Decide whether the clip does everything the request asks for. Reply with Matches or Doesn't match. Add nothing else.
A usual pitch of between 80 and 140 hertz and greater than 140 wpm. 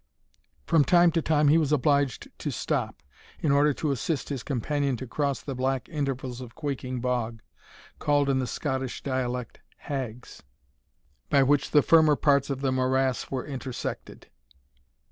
Matches